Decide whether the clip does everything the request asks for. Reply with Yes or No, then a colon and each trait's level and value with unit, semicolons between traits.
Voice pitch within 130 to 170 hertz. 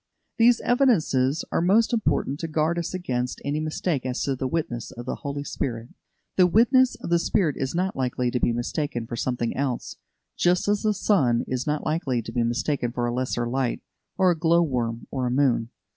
Yes: medium, 140 Hz